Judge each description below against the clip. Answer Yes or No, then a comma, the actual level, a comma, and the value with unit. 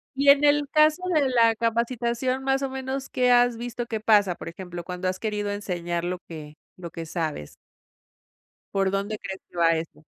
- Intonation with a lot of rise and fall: Yes, wide, 6.3 semitones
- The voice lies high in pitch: Yes, high, 215 Hz